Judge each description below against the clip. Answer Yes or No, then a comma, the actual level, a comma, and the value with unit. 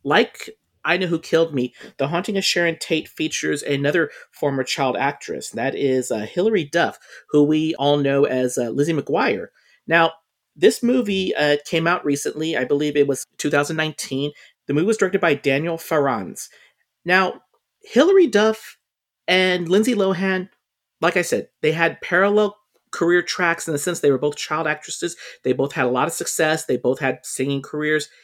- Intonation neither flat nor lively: Yes, average, 4.5 semitones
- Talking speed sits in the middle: Yes, average, 175 wpm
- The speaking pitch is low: No, medium, 160 Hz